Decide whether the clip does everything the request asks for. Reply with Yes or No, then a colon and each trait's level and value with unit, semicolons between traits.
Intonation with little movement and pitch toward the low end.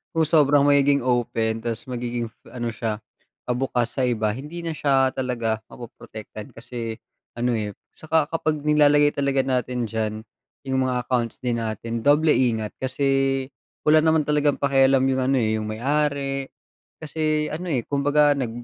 No: average, 3.8 semitones; low, 130 Hz